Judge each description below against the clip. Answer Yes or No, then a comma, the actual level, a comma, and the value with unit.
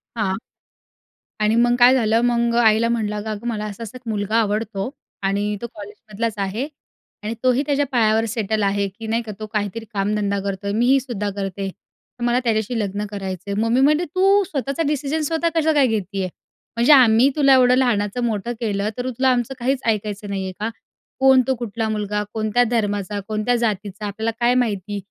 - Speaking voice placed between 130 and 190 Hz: No, high, 220 Hz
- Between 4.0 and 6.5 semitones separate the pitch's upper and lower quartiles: No, average, 3.0 semitones